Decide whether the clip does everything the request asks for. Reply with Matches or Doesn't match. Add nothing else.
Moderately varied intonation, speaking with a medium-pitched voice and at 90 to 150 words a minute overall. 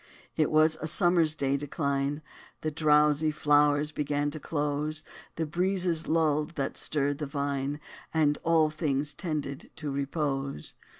Doesn't match